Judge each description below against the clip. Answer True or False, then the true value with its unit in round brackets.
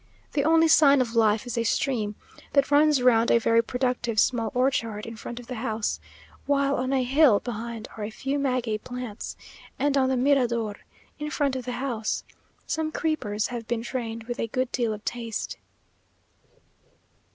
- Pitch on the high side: True (245 Hz)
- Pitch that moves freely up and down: False (3.2 semitones)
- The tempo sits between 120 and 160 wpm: False (175 wpm)